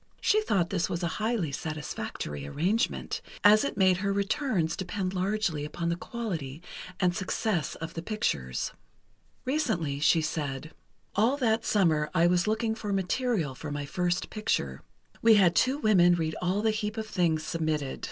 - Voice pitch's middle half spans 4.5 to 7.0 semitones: Yes, average, 5.2 semitones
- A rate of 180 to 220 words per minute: No, average, 160 wpm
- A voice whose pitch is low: No, medium, 180 Hz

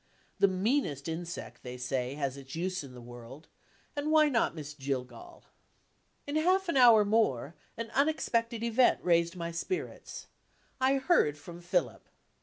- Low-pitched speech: No, medium, 175 Hz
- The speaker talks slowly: No, average, 150 wpm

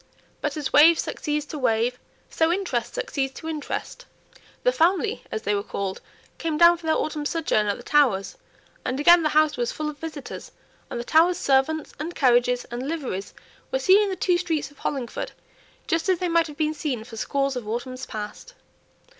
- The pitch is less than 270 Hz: No, very high, 300 Hz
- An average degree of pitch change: Yes, average, 5.0 semitones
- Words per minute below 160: No, average, 195 wpm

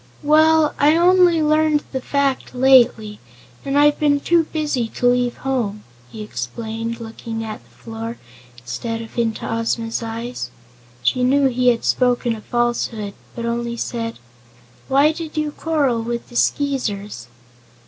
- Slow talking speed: No, average, 145 wpm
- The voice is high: Yes, high, 245 Hz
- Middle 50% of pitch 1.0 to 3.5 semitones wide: No, average, 4.2 semitones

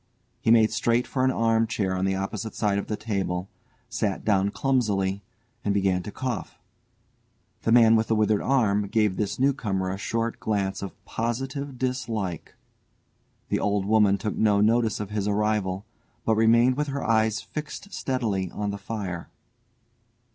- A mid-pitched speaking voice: No, low, 110 Hz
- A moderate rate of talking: Yes, average, 165 wpm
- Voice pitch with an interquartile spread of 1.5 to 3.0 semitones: Yes, average, 2.7 semitones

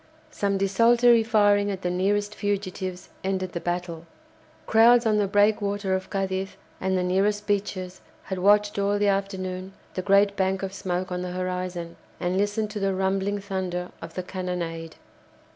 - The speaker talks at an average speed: Yes, average, 160 wpm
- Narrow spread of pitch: Yes, narrow, 1.9 semitones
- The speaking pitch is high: Yes, high, 195 Hz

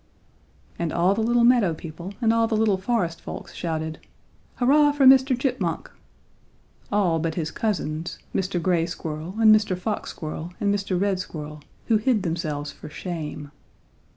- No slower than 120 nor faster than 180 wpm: Yes, average, 155 wpm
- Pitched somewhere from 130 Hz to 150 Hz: No, medium, 185 Hz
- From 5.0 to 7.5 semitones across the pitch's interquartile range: Yes, average, 5.3 semitones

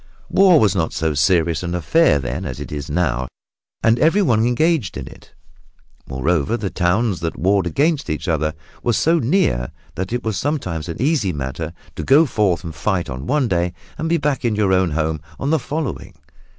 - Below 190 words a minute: No, average, 195 wpm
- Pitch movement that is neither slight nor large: No, wide, 8.4 semitones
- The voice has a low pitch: Yes, very low, 95 Hz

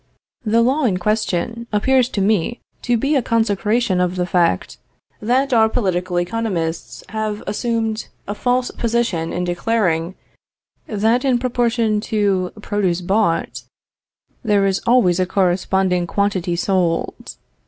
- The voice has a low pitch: No, high, 210 Hz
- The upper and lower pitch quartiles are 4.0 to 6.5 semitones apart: Yes, average, 4.3 semitones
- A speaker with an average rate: No, slow, 130 wpm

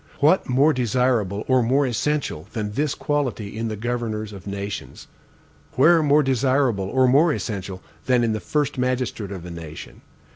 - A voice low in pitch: Yes, low, 120 Hz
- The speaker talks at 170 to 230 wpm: No, average, 160 wpm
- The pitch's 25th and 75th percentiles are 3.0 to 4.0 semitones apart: No, average, 4.7 semitones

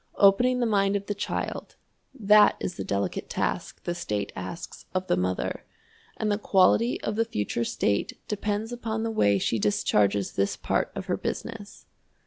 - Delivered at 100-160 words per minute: No, average, 170 wpm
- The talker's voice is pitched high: Yes, high, 195 Hz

